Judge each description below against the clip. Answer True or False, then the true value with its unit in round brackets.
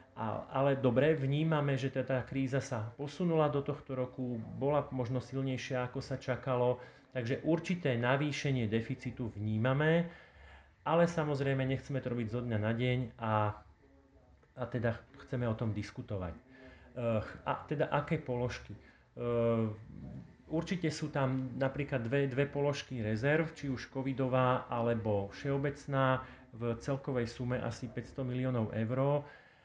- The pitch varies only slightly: False (3.1 semitones)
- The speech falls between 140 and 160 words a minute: False (125 wpm)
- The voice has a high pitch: False (130 Hz)